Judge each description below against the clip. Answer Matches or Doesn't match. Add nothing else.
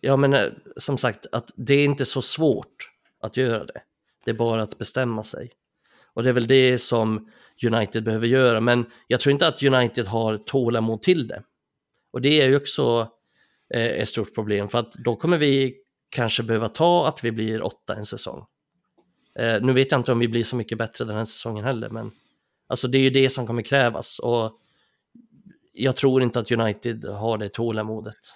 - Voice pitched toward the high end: Doesn't match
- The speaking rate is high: Matches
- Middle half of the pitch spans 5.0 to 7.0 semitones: Doesn't match